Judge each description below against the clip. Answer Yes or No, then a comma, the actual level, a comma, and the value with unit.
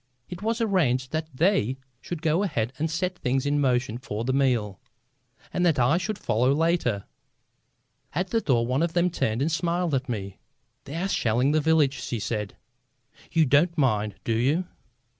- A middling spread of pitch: No, wide, 5.9 semitones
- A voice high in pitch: No, medium, 140 Hz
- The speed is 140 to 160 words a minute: No, average, 180 wpm